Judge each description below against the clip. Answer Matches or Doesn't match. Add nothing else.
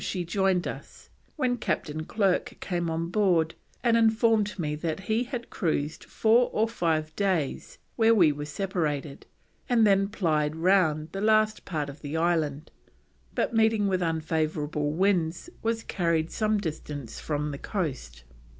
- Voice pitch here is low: Doesn't match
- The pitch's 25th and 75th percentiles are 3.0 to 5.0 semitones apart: Doesn't match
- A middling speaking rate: Matches